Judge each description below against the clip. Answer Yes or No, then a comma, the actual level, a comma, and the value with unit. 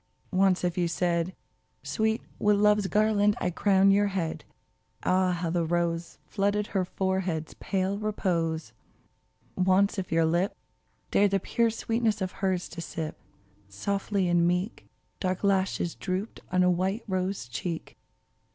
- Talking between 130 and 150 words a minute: Yes, average, 140 wpm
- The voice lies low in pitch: No, medium, 185 Hz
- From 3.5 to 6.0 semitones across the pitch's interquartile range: No, narrow, 2.5 semitones